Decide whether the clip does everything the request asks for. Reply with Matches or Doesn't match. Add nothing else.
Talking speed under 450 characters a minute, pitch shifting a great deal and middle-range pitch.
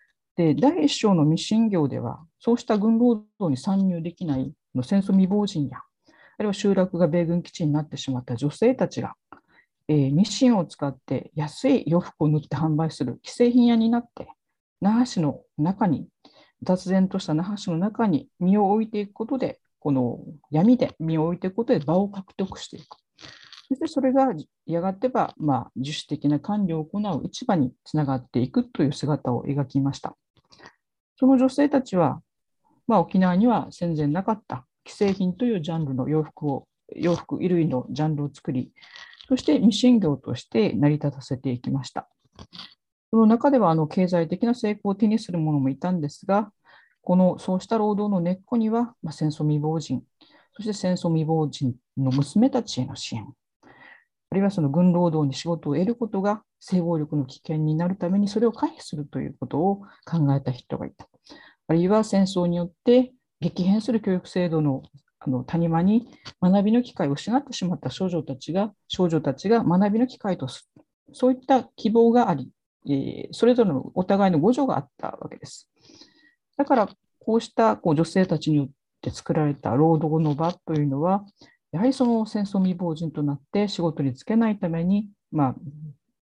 Matches